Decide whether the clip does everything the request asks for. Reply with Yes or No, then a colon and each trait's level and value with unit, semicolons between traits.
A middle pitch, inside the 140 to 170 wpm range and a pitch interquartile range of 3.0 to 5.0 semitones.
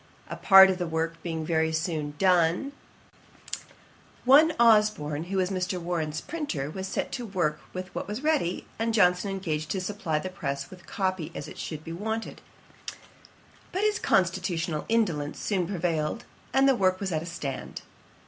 Yes: medium, 180 Hz; average, 165 wpm; average, 4.3 semitones